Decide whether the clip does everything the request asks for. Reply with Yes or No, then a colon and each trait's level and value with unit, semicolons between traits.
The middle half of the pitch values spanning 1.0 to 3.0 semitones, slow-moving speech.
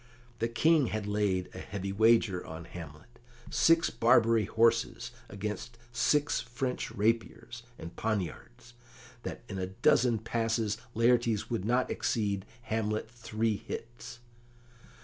Yes: narrow, 2.6 semitones; slow, 120 wpm